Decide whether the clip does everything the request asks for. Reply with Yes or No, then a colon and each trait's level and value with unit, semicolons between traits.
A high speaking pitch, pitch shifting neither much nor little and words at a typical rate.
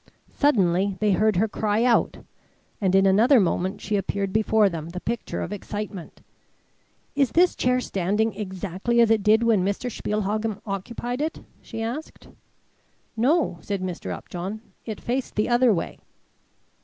Yes: high, 210 Hz; average, 3.4 semitones; average, 150 wpm